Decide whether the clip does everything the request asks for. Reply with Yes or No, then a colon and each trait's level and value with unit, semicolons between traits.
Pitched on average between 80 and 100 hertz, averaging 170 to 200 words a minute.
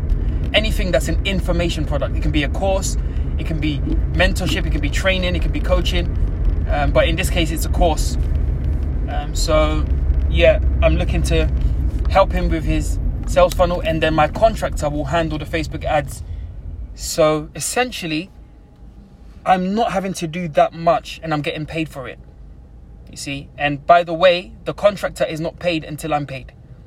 Yes: very low, 85 Hz; average, 180 wpm